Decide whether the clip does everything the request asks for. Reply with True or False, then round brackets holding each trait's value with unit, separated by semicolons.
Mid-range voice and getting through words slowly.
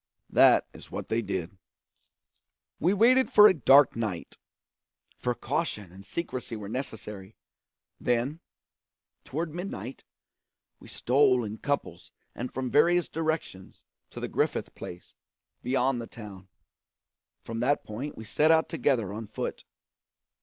False (125 Hz; 130 wpm)